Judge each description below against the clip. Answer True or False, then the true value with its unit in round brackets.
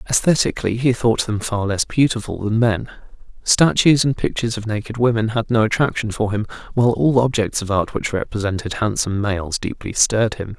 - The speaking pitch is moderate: False (110 Hz)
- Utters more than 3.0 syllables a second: True (5.6 syllables/s)